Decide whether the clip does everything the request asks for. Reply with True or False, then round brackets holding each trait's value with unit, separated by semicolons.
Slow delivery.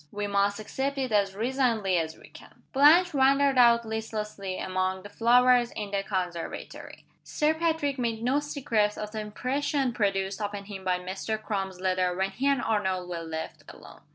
False (175 wpm)